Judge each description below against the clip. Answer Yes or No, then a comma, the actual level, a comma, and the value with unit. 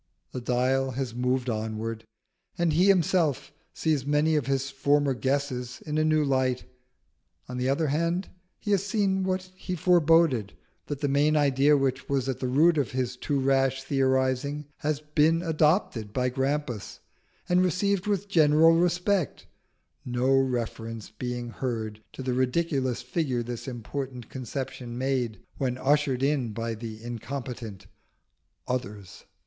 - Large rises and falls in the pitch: No, average, 3.7 semitones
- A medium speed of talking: Yes, average, 145 wpm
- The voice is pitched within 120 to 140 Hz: Yes, low, 135 Hz